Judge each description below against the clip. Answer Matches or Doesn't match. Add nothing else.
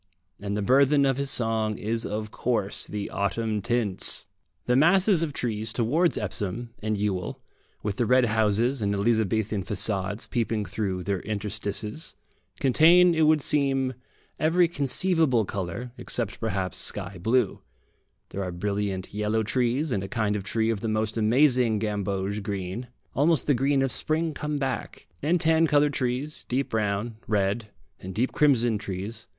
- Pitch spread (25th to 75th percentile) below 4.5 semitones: Doesn't match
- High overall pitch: Doesn't match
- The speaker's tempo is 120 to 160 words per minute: Matches